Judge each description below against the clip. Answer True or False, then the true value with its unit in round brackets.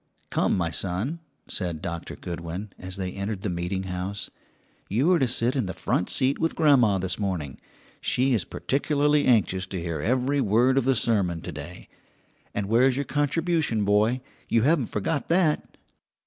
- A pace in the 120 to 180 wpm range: True (170 wpm)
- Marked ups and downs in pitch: True (6.6 semitones)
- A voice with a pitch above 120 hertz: False (105 Hz)